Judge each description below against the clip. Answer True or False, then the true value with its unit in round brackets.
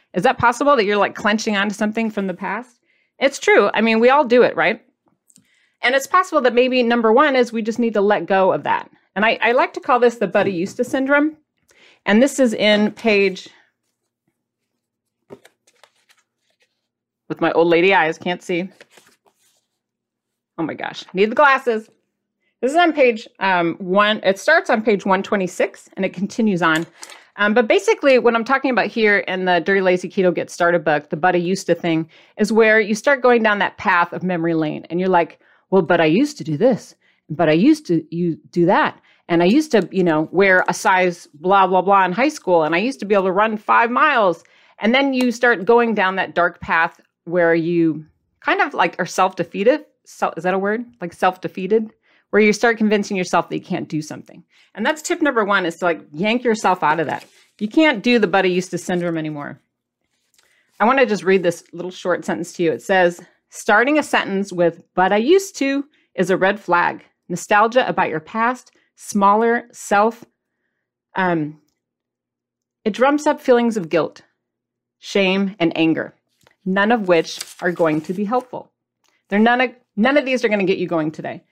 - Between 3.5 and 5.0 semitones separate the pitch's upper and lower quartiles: False (5.4 semitones)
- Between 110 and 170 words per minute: False (200 wpm)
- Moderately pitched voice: False (195 Hz)